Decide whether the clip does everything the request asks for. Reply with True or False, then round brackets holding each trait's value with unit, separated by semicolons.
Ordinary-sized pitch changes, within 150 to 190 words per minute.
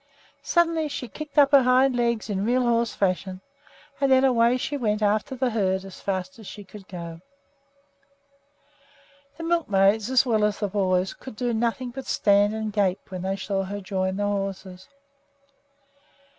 True (4.6 semitones; 170 wpm)